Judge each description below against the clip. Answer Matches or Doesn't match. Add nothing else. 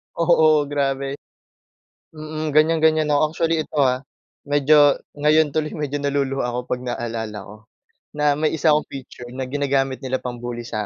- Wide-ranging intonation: Doesn't match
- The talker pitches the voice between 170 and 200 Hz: Doesn't match